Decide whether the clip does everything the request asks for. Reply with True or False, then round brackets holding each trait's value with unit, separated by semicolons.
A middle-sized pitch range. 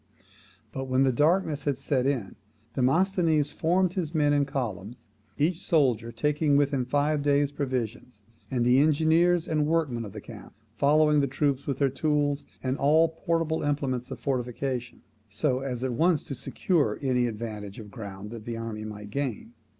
True (3.9 semitones)